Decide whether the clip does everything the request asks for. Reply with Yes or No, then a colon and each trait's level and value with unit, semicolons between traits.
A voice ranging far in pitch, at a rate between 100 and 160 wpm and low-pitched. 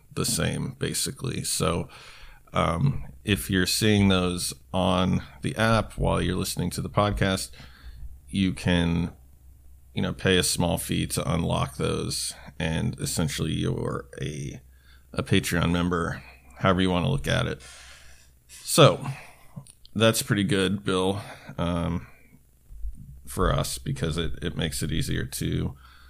Yes: wide, 6.6 semitones; slow, 135 wpm; very low, 85 Hz